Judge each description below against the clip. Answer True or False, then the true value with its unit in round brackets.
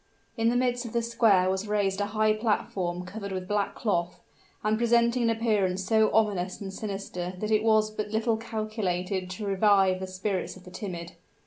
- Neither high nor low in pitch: False (210 Hz)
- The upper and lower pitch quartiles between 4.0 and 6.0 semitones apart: False (2.8 semitones)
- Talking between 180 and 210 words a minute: True (190 wpm)